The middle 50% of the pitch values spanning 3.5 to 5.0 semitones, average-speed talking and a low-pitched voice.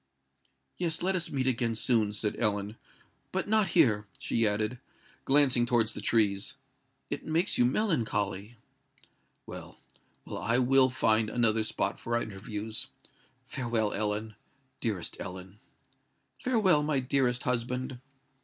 No: average, 3.9 semitones; slow, 115 wpm; low, 120 Hz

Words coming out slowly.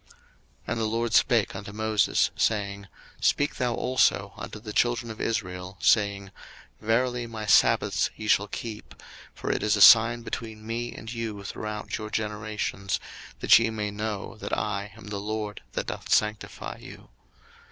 No: average, 165 wpm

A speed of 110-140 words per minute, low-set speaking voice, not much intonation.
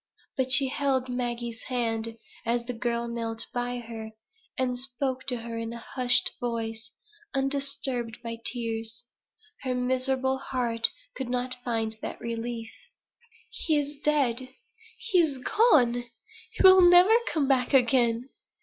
No: slow, 135 wpm; high, 245 Hz; narrow, 2.3 semitones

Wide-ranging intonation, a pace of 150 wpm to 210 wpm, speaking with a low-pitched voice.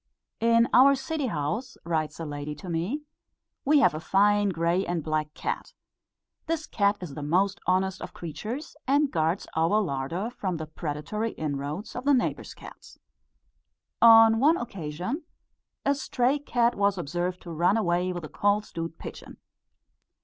No: wide, 6.3 semitones; average, 155 wpm; high, 190 Hz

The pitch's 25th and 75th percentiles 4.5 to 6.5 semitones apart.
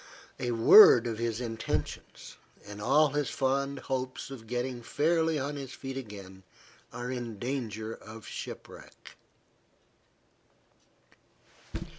No: average, 3.4 semitones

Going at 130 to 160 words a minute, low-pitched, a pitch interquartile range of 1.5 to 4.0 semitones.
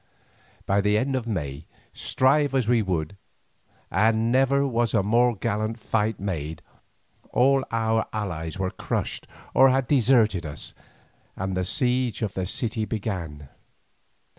No: average, 140 wpm; low, 110 Hz; average, 4.6 semitones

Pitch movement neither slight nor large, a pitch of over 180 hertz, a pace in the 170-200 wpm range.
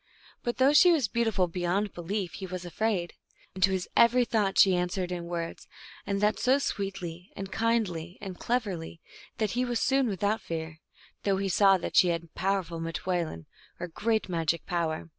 Yes: average, 3.9 semitones; high, 190 Hz; average, 180 wpm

